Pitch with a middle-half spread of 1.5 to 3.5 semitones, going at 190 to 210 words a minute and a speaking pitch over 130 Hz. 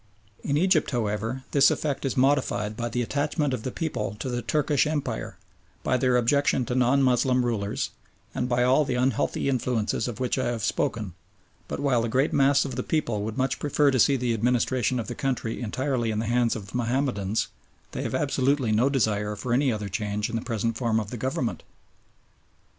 No: average, 3.2 semitones; average, 200 wpm; low, 125 Hz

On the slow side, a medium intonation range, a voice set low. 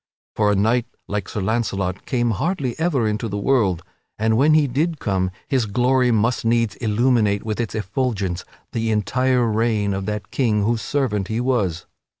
No: average, 170 wpm; average, 3.4 semitones; low, 110 Hz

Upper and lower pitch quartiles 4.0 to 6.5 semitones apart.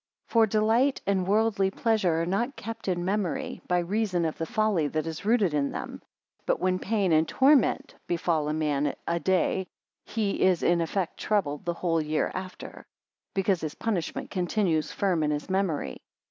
Yes: average, 4.3 semitones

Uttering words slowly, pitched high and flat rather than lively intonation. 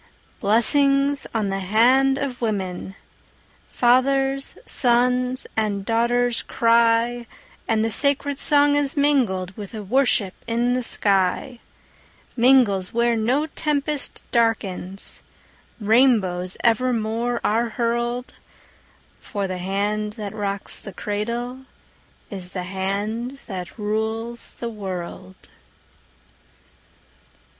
No: slow, 100 wpm; high, 230 Hz; average, 3.8 semitones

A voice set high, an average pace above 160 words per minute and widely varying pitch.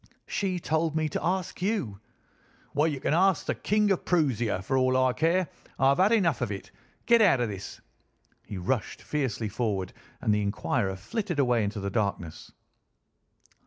No: low, 135 Hz; average, 170 wpm; wide, 9.0 semitones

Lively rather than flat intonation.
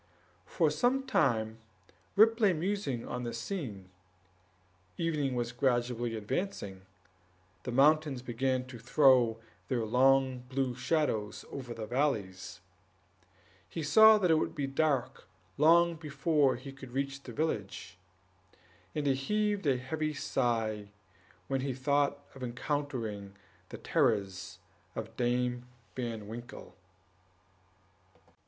No: average, 4.2 semitones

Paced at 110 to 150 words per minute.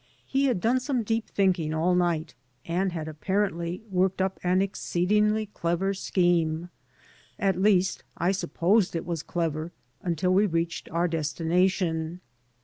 Yes: average, 140 wpm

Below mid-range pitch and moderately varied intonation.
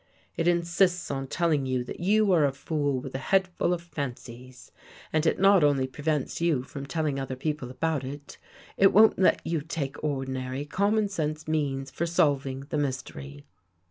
No: medium, 145 Hz; average, 4.2 semitones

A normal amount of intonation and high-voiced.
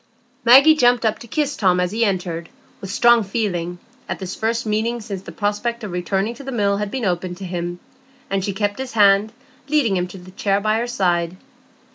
Yes: average, 4.2 semitones; high, 205 Hz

